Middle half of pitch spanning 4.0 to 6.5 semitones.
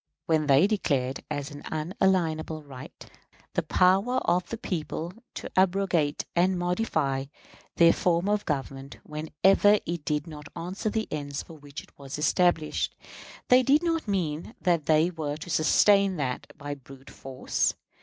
Yes: average, 4.5 semitones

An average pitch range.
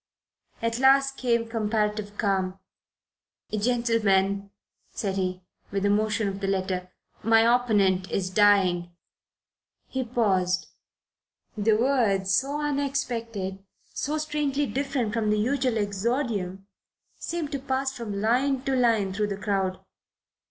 Yes: average, 4.6 semitones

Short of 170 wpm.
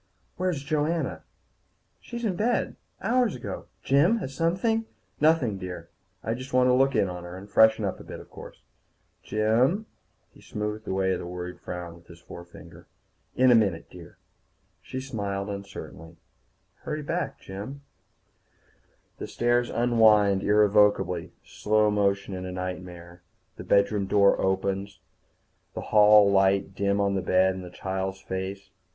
Yes: average, 150 wpm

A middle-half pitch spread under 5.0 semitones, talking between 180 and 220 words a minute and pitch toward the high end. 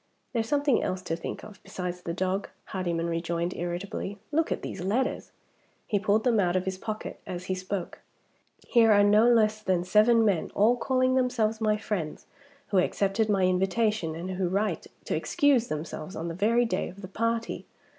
Yes: average, 3.7 semitones; average, 185 wpm; high, 200 Hz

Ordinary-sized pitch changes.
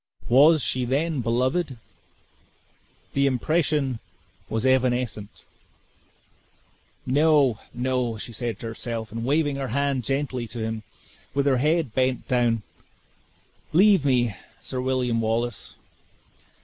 Yes: average, 3.2 semitones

